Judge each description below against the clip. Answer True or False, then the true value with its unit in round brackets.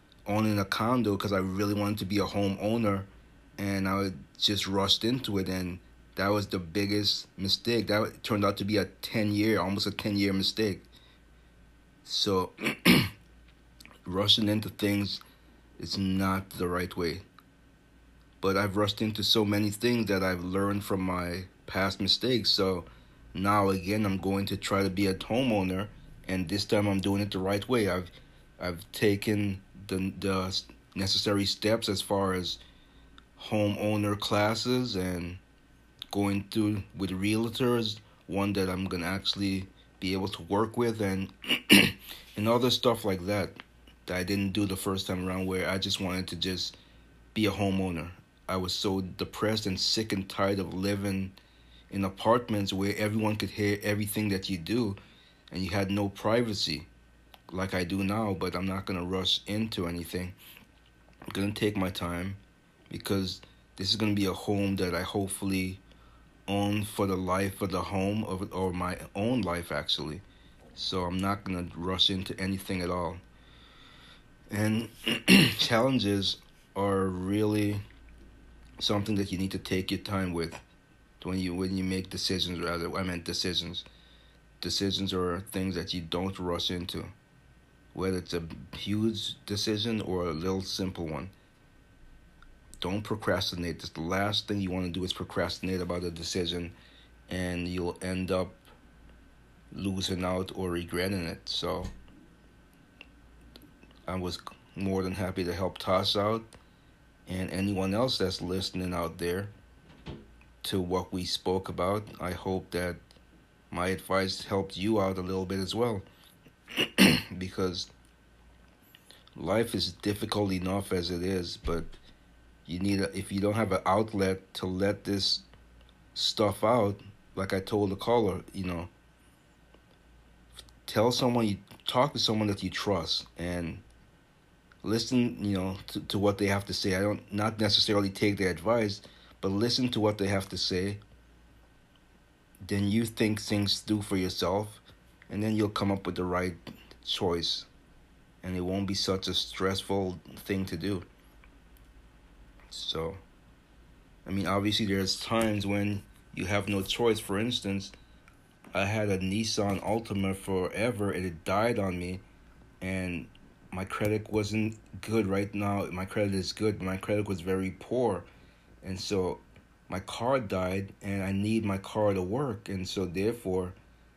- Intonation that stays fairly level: True (2.1 semitones)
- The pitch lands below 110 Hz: True (95 Hz)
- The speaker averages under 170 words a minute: True (155 wpm)